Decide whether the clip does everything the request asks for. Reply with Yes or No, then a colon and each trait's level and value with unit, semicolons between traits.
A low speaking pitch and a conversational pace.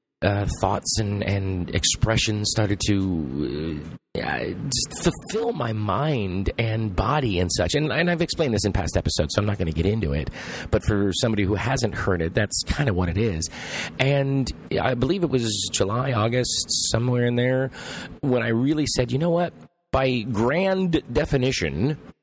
Yes: low, 110 Hz; average, 175 wpm